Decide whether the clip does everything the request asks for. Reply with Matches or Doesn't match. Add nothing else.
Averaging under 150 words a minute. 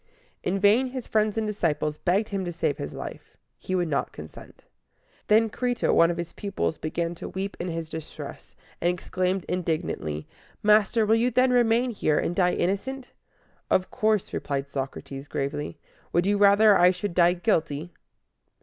Doesn't match